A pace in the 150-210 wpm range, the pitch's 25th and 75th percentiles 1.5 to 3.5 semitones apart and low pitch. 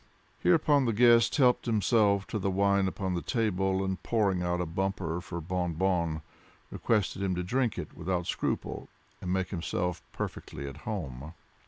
Yes: average, 165 wpm; average, 3.0 semitones; very low, 95 Hz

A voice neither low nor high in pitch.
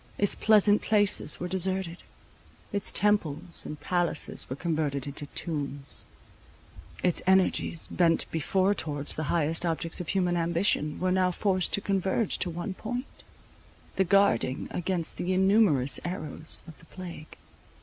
Yes: medium, 175 Hz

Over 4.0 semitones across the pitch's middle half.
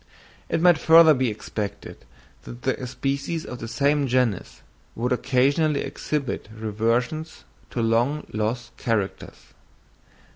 Yes: average, 4.4 semitones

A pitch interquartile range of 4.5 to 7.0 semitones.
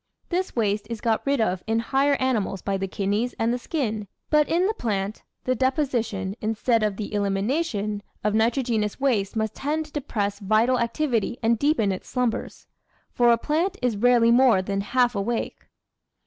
No: average, 4.0 semitones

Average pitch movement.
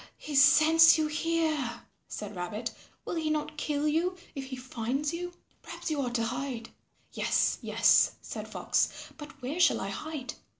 Yes: average, 4.1 semitones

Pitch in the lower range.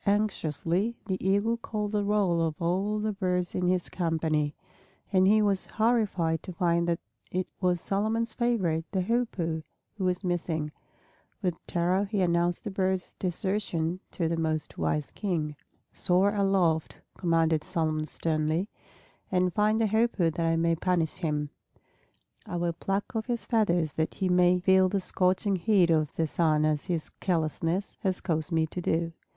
No: medium, 180 Hz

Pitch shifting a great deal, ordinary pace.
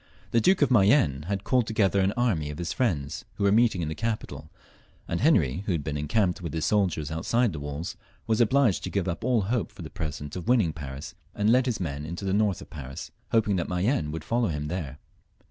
No: wide, 6.6 semitones; fast, 230 wpm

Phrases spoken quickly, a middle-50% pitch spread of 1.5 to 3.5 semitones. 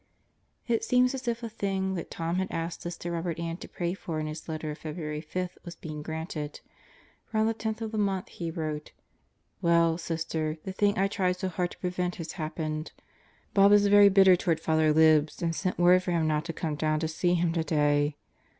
Yes: fast, 215 wpm; average, 3.2 semitones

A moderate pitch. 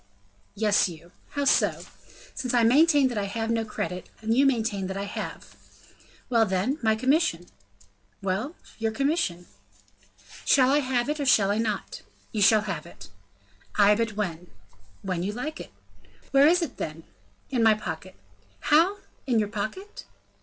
No: high, 225 Hz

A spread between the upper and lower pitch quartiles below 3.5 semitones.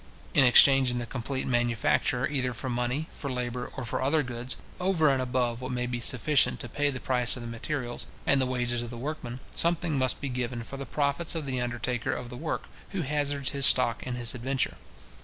Yes: narrow, 2.4 semitones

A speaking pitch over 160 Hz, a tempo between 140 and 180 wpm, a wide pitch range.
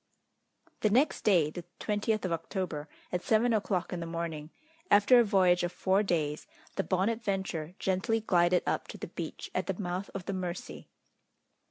No: medium, 185 Hz; average, 170 wpm; average, 3.2 semitones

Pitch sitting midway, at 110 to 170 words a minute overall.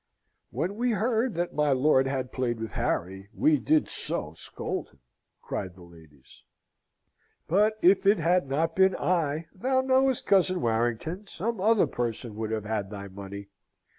Yes: medium, 150 Hz; average, 160 wpm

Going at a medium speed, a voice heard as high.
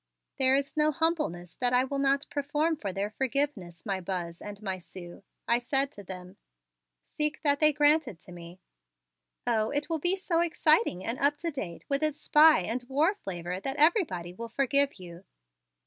Yes: average, 185 wpm; very high, 265 Hz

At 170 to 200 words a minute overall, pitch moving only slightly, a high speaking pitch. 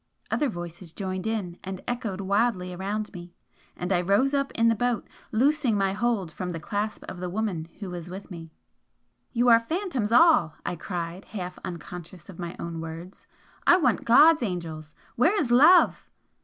No: average, 175 wpm; average, 5.2 semitones; high, 195 Hz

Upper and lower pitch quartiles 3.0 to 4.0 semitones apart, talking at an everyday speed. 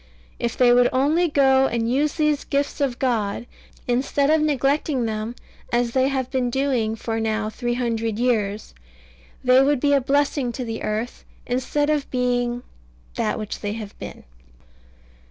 Yes: average, 3.4 semitones; average, 160 wpm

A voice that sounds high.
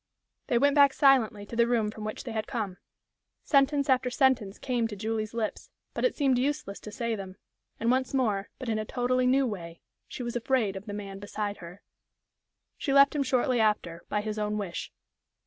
Yes: high, 230 Hz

